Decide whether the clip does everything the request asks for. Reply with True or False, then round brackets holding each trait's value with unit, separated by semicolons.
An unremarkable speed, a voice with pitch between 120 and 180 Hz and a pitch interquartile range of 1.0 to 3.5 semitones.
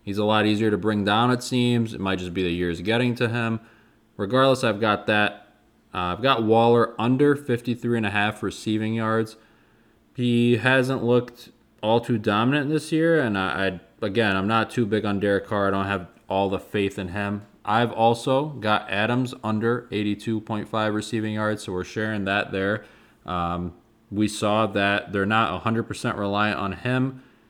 False (180 wpm; 110 Hz; 2.7 semitones)